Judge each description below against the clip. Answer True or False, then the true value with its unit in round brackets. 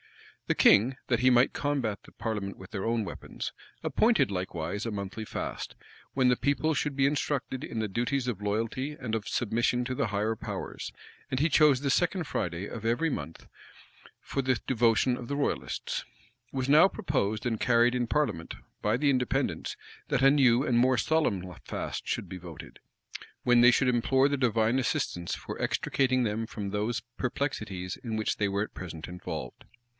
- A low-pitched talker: True (120 Hz)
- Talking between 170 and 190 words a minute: True (180 wpm)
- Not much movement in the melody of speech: False (4.2 semitones)